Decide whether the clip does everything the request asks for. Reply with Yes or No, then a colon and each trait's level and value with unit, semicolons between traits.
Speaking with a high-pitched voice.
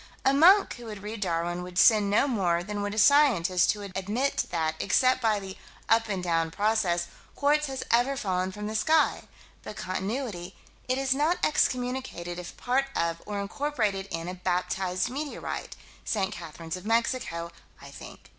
Yes: high, 205 Hz